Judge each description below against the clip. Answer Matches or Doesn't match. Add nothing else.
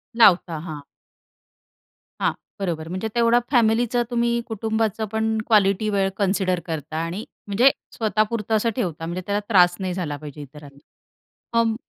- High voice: Matches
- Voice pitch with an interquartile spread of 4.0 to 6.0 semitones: Matches